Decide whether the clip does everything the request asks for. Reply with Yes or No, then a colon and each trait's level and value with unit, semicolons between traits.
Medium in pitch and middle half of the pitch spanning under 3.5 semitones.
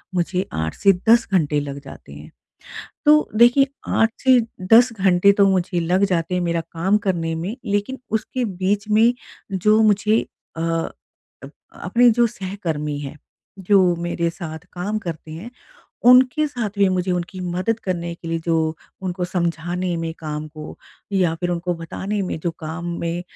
No: medium, 180 Hz; average, 3.8 semitones